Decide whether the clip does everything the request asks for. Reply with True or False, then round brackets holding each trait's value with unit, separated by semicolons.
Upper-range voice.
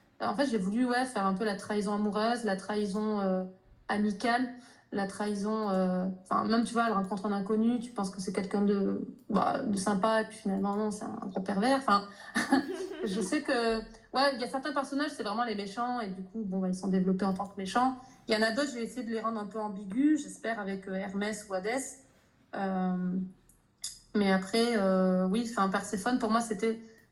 True (215 Hz)